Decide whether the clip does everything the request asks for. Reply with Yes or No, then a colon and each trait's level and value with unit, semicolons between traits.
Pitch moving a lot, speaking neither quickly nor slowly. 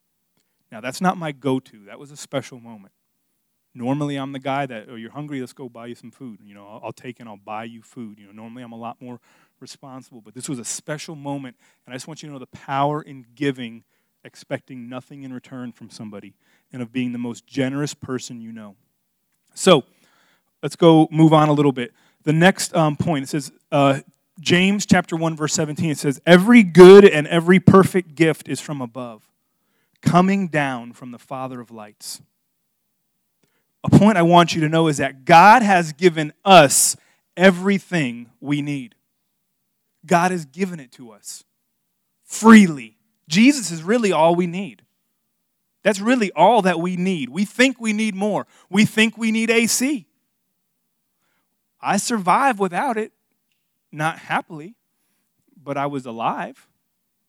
Yes: wide, 6.9 semitones; average, 175 wpm